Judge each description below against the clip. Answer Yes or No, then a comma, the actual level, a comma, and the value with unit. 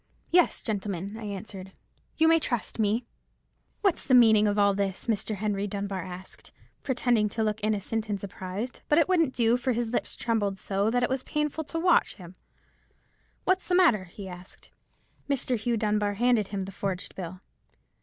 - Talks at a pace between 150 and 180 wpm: Yes, average, 175 wpm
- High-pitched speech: Yes, high, 215 Hz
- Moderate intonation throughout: Yes, average, 3.8 semitones